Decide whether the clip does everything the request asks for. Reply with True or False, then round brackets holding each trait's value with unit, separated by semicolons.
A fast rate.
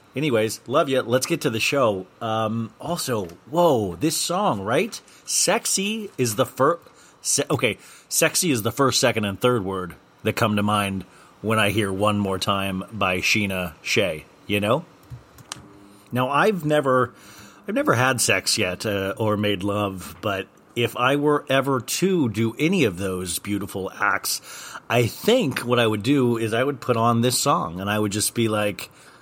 False (175 wpm)